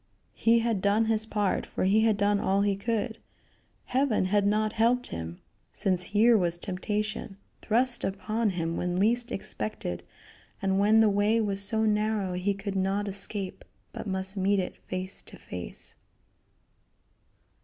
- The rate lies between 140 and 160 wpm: Yes, average, 155 wpm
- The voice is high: Yes, high, 205 Hz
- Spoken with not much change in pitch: Yes, narrow, 2.3 semitones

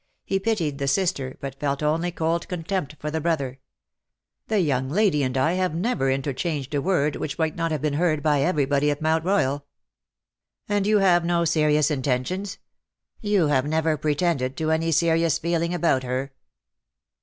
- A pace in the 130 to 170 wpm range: No, average, 190 wpm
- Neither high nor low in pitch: Yes, medium, 155 Hz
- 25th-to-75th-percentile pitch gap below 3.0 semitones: No, average, 3.6 semitones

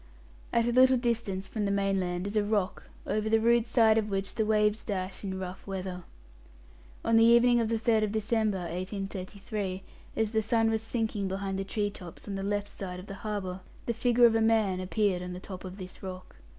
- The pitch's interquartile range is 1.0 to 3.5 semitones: Yes, average, 2.8 semitones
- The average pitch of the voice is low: No, high, 205 Hz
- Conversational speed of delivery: No, fast, 210 wpm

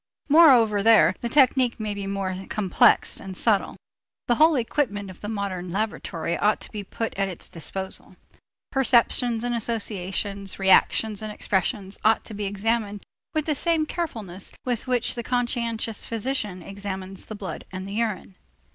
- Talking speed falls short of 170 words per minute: Yes, average, 155 wpm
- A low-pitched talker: No, high, 210 Hz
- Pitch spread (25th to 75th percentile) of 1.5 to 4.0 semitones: Yes, average, 3.4 semitones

